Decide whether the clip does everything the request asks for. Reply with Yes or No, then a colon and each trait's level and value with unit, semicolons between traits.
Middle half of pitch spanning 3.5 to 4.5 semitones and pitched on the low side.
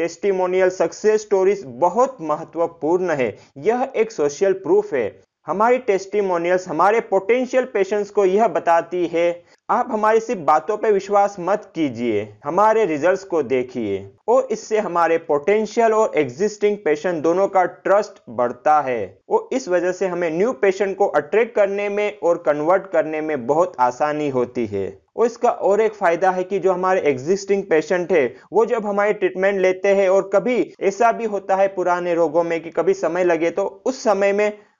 No: average, 3.9 semitones; high, 190 Hz